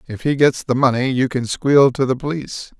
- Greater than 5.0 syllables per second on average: Yes, 5.3 syllables/s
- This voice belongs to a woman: No, male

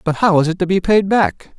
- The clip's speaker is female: No, male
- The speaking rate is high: Yes, fast, 300 wpm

